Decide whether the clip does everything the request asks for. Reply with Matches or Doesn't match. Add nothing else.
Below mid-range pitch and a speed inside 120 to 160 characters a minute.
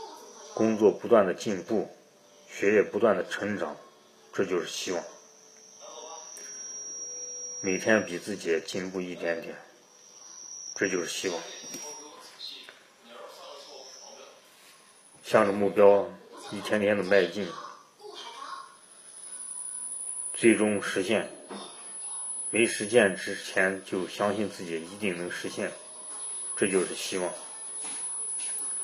Matches